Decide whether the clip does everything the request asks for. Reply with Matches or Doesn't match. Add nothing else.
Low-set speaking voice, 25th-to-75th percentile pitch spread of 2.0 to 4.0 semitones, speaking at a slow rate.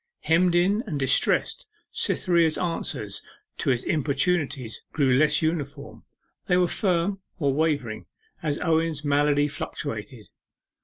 Doesn't match